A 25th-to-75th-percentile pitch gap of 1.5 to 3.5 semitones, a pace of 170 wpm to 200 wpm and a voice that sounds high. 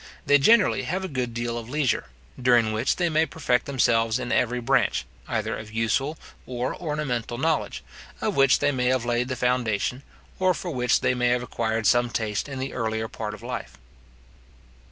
No: average, 3.0 semitones; average, 185 wpm; low, 125 Hz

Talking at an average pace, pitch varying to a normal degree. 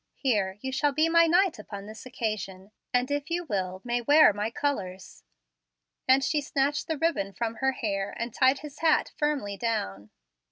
No: average, 175 wpm; wide, 6.3 semitones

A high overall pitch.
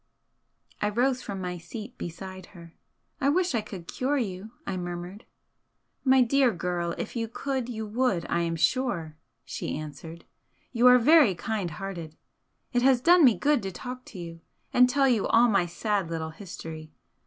Yes: high, 210 Hz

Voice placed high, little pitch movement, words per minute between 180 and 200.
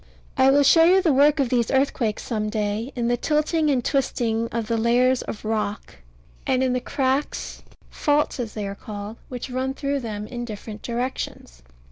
No: high, 245 Hz; average, 3.7 semitones; average, 185 wpm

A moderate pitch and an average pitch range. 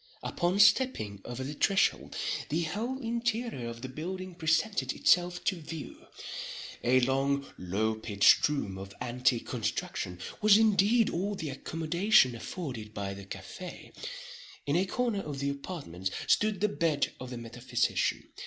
No: medium, 150 Hz; wide, 8.4 semitones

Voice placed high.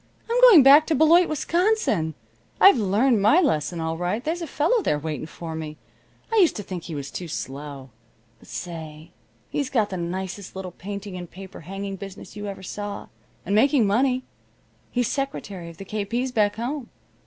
Yes: high, 200 Hz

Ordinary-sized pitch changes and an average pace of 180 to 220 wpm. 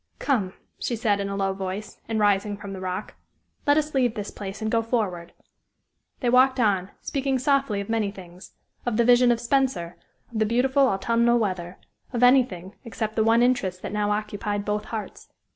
Yes: average, 3.6 semitones; average, 190 wpm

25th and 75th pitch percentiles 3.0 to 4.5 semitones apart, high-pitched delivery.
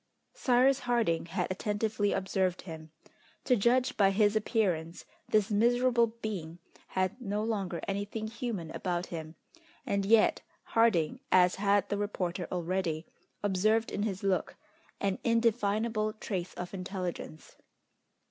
Yes: average, 3.5 semitones; high, 200 Hz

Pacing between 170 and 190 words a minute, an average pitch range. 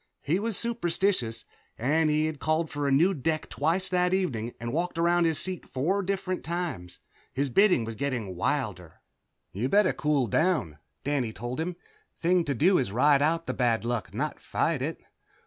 No: average, 180 wpm; wide, 6.1 semitones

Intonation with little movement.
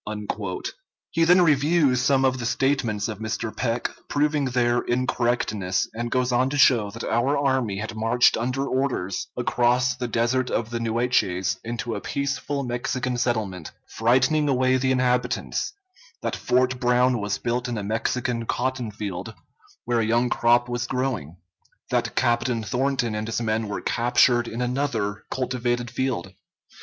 Yes: narrow, 2.3 semitones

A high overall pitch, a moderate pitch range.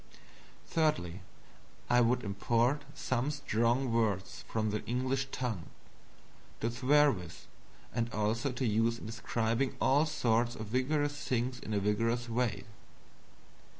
No: low, 120 Hz; average, 3.0 semitones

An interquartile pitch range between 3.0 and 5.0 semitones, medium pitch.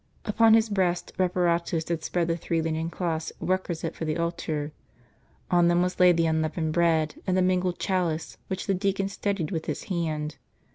No: narrow, 2.4 semitones; medium, 170 Hz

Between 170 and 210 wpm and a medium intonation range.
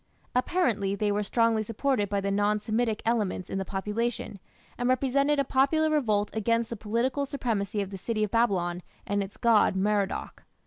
Yes: average, 175 wpm; average, 3.3 semitones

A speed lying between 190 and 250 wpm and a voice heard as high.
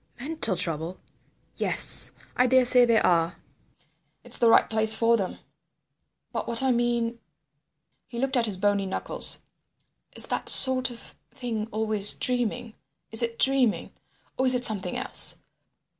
No: average, 145 wpm; high, 230 Hz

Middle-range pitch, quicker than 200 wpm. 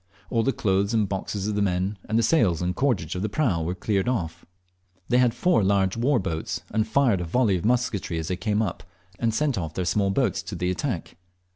No: low, 100 Hz; fast, 230 wpm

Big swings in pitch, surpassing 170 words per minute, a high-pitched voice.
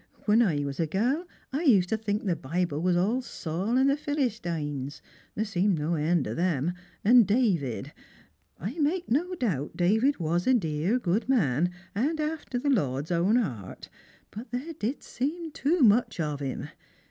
Yes: wide, 7.9 semitones; average, 180 wpm; high, 205 Hz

